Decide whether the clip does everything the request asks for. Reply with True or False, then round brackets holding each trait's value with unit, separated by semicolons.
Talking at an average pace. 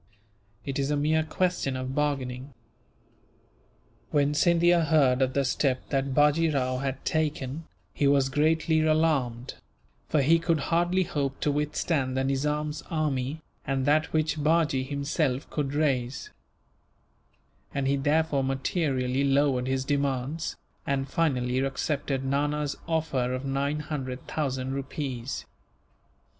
False (125 wpm)